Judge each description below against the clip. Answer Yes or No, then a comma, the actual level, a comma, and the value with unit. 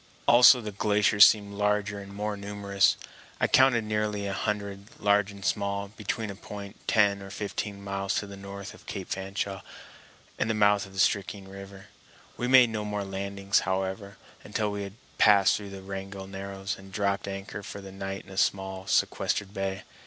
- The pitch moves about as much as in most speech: No, narrow, 1.1 semitones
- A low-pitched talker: Yes, low, 100 Hz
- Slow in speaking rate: No, average, 180 wpm